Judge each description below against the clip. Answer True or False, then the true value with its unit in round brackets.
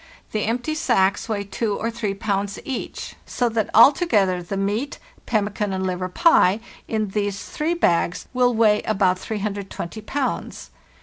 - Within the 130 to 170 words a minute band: True (150 wpm)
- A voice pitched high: True (210 Hz)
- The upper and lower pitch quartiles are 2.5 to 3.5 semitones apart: True (3.0 semitones)